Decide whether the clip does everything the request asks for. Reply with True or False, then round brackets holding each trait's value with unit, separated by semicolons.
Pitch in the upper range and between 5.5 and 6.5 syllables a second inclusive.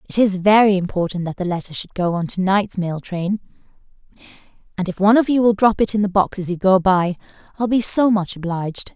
True (195 Hz; 5.9 syllables/s)